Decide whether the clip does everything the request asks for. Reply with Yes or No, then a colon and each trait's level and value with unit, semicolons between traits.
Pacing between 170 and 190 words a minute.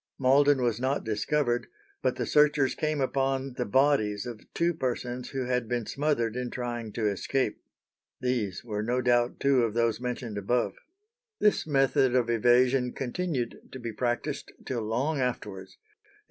No: average, 155 wpm